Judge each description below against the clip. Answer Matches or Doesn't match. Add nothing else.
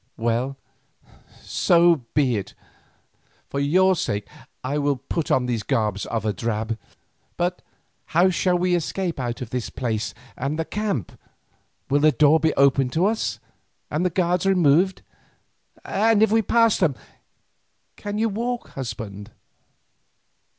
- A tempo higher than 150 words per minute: Doesn't match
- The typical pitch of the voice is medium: Matches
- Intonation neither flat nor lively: Doesn't match